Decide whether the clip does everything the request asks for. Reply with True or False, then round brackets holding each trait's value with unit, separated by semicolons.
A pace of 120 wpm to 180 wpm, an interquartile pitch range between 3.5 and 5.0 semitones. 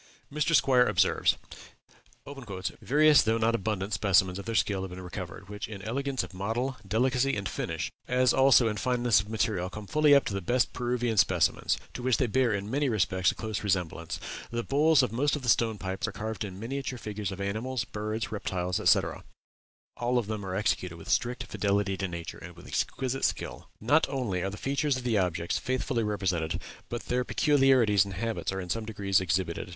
False (200 wpm; 4.6 semitones)